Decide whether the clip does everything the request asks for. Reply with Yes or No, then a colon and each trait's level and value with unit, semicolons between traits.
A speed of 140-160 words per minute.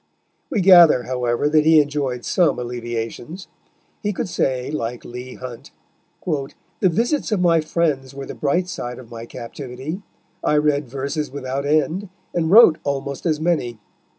Yes: average, 150 wpm